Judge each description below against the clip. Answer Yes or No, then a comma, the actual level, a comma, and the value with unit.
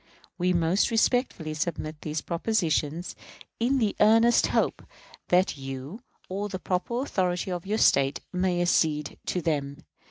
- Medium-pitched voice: Yes, medium, 180 Hz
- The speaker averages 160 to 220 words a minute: No, slow, 135 wpm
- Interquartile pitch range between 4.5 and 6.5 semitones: Yes, average, 5.1 semitones